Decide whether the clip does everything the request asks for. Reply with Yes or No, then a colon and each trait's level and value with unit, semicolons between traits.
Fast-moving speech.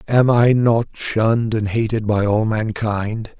No: average, 160 wpm